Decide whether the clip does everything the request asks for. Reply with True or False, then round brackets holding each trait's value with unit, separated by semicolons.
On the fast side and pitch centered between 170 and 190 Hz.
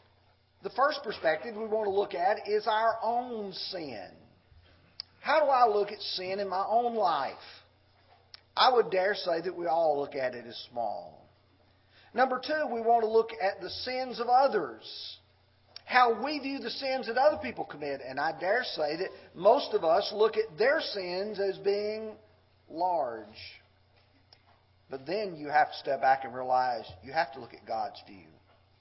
False (175 wpm; 185 Hz)